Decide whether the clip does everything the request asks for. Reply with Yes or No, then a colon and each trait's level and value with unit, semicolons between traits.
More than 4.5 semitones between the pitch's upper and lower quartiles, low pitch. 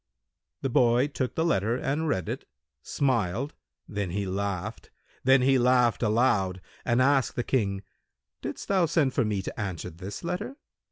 Yes: average, 5.2 semitones; low, 120 Hz